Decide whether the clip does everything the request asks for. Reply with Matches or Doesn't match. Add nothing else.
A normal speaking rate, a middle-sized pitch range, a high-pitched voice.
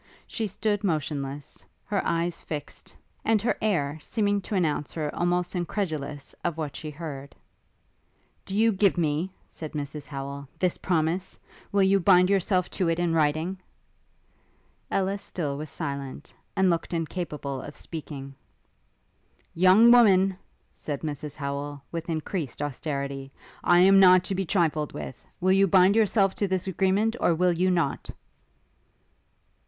Doesn't match